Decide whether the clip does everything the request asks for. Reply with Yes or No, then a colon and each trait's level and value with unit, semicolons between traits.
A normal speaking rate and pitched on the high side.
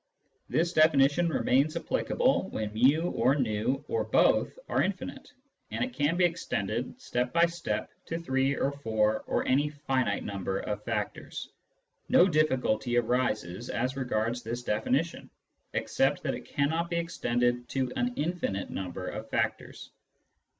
No: average, 145 wpm; low, 130 Hz